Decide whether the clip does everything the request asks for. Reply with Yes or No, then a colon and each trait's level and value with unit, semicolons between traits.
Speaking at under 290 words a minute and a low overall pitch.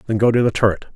No: fast, 315 wpm; low, 110 Hz